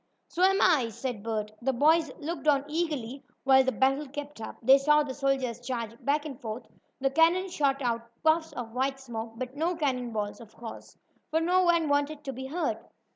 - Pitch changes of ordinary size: Yes, average, 4.1 semitones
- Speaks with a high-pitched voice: Yes, very high, 270 Hz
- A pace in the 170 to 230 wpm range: Yes, average, 200 wpm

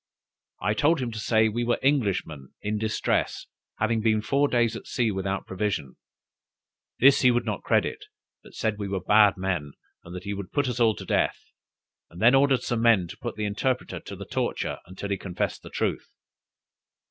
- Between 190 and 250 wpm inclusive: Yes, average, 195 wpm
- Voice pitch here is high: No, low, 110 Hz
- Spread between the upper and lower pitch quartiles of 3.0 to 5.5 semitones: Yes, average, 3.6 semitones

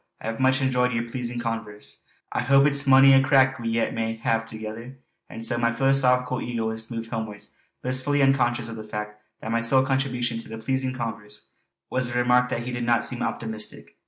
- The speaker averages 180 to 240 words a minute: Yes, average, 200 wpm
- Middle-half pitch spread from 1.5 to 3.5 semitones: Yes, narrow, 2.4 semitones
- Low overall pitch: Yes, low, 120 Hz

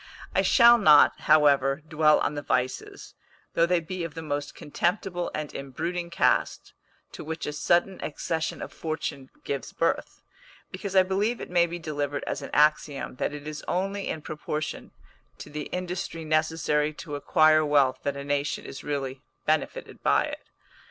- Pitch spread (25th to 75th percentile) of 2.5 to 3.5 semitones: Yes, average, 2.9 semitones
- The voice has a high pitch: No, medium, 155 Hz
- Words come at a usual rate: Yes, average, 165 wpm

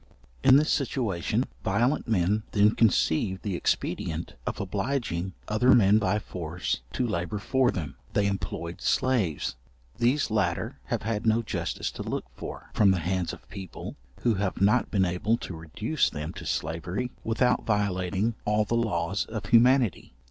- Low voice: Yes, low, 105 Hz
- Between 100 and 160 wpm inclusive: Yes, average, 155 wpm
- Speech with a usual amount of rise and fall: Yes, average, 4.4 semitones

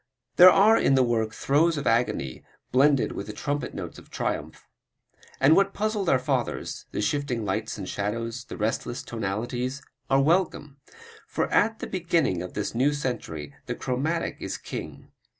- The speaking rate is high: No, average, 165 wpm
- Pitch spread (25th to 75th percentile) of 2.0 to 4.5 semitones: No, average, 5.2 semitones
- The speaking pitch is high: No, low, 130 Hz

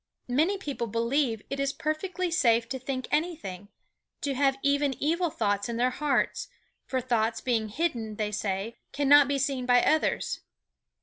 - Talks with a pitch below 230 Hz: No, very high, 260 Hz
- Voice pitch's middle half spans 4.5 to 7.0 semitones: No, average, 4.1 semitones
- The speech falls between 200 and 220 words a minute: No, average, 160 wpm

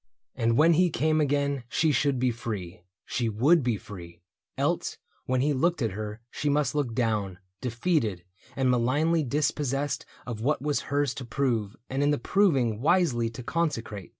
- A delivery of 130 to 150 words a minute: No, average, 175 wpm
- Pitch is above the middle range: No, low, 130 Hz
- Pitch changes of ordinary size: Yes, average, 4.5 semitones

